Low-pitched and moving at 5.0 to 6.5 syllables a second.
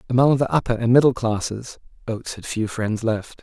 Yes: low, 120 Hz; 5.4 syllables/s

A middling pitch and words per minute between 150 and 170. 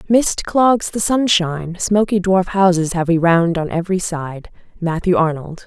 Yes: medium, 180 Hz; average, 160 wpm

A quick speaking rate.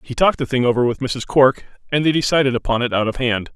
Yes: fast, 270 wpm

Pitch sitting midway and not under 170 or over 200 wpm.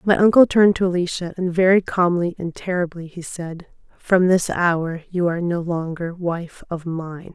Yes: medium, 175 Hz; average, 180 wpm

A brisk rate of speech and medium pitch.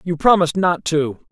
No: average, 185 wpm; medium, 165 Hz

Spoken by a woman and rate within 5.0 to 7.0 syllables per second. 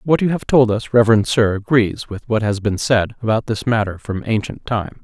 No: male; 5.2 syllables/s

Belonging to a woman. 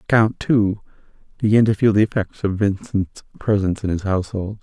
No: male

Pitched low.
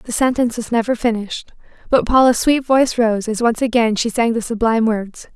No: high, 230 Hz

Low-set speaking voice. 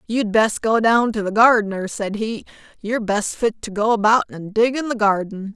No: high, 215 Hz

